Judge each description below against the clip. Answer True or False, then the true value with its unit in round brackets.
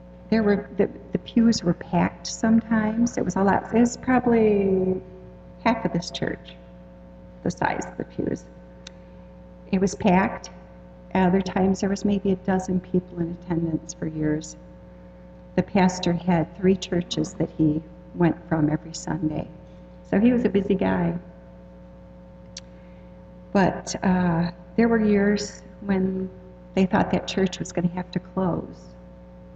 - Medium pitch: True (175 Hz)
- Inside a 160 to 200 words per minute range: False (145 wpm)